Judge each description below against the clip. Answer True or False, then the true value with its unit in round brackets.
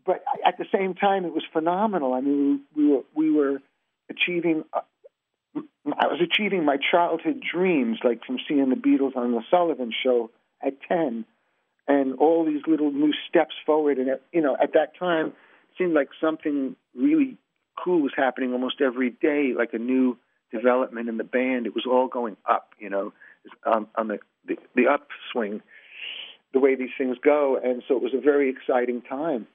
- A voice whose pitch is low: False (145 Hz)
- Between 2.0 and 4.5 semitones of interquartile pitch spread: False (5.2 semitones)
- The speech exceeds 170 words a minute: True (185 wpm)